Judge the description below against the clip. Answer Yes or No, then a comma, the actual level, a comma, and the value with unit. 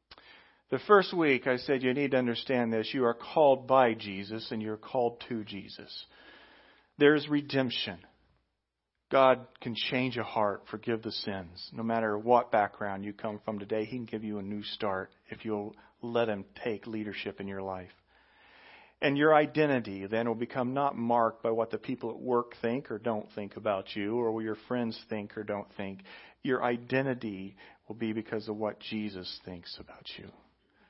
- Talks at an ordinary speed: Yes, average, 180 wpm